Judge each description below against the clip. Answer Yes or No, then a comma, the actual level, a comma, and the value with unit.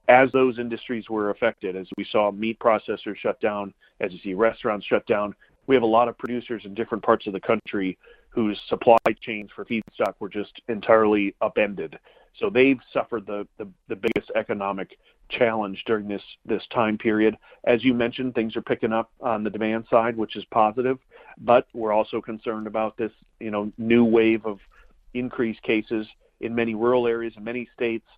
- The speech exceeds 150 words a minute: Yes, average, 185 wpm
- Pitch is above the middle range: No, low, 115 Hz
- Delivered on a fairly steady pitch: Yes, narrow, 2.0 semitones